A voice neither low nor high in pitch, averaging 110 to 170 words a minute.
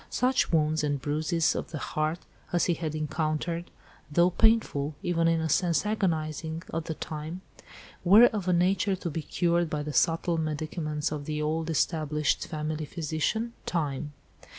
Yes: medium, 160 Hz; average, 160 wpm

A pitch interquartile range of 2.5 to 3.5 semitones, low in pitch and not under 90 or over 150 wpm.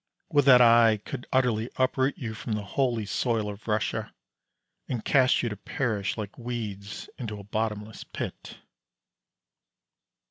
Yes: average, 2.8 semitones; low, 115 Hz; average, 140 wpm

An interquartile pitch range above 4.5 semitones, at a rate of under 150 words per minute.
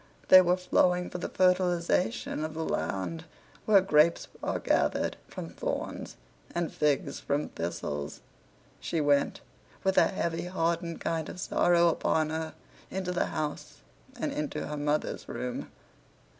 No: average, 3.1 semitones; average, 140 wpm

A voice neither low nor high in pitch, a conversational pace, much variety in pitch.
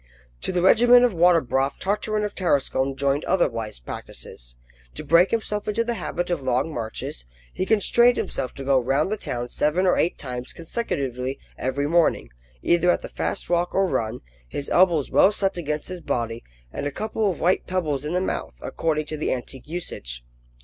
Yes: medium, 160 Hz; average, 190 wpm; wide, 6.0 semitones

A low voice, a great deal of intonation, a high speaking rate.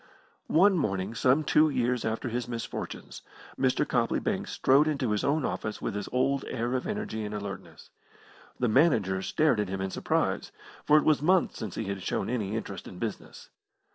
No: low, 120 Hz; wide, 5.8 semitones; average, 185 wpm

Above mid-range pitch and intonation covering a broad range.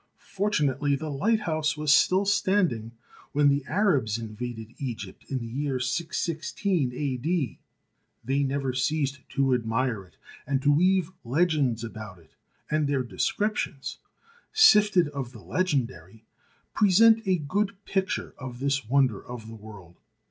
No: medium, 140 Hz; wide, 6.2 semitones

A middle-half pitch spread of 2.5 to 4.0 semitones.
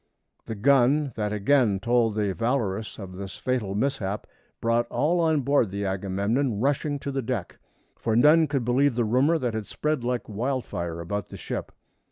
No: average, 5.3 semitones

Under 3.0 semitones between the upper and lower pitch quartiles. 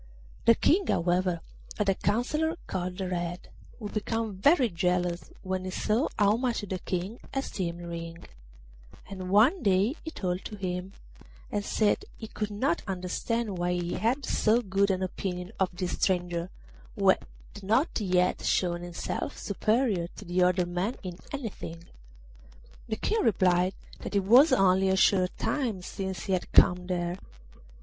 No: average, 3.3 semitones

